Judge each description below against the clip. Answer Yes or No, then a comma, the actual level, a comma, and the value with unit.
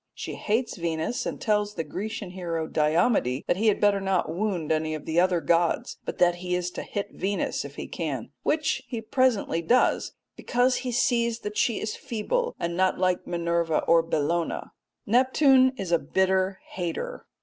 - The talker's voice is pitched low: No, high, 190 Hz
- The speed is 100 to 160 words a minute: No, average, 180 wpm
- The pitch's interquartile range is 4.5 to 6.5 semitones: Yes, average, 4.9 semitones